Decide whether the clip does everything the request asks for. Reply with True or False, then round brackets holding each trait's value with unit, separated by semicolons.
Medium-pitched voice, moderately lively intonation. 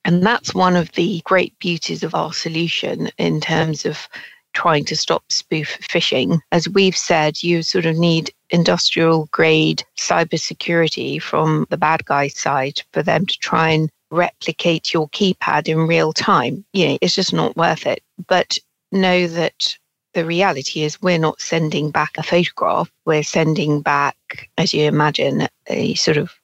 False (165 Hz; 2.1 semitones)